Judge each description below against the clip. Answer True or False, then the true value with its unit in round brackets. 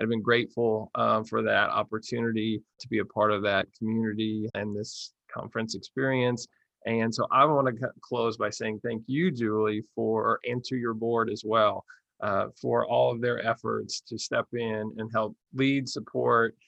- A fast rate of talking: False (175 wpm)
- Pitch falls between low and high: False (115 Hz)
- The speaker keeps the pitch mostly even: True (1.7 semitones)